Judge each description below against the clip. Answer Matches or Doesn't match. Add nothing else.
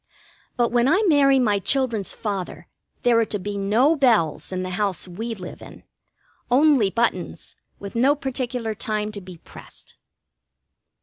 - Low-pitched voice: Doesn't match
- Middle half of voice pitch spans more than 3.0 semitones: Matches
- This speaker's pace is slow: Doesn't match